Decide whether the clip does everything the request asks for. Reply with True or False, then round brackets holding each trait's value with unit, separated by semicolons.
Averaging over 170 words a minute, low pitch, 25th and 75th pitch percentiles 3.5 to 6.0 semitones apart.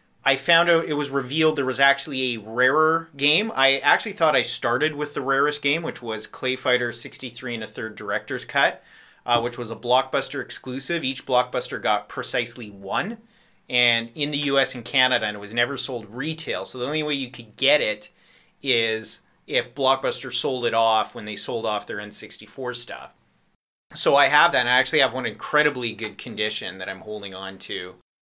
True (195 wpm; 125 Hz; 3.9 semitones)